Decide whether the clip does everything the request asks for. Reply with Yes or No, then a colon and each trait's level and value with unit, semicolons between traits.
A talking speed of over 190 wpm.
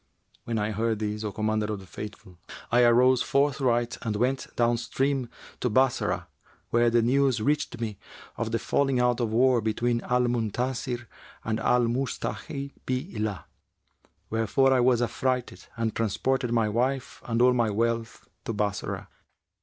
No: average, 155 wpm